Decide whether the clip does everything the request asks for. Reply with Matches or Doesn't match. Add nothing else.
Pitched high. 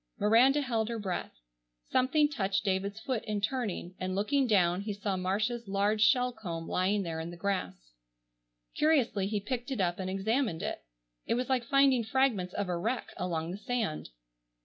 Matches